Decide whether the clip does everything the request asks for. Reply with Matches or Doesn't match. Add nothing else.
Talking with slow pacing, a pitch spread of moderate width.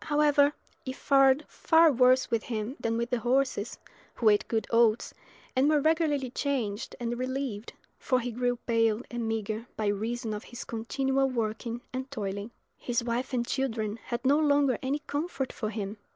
Doesn't match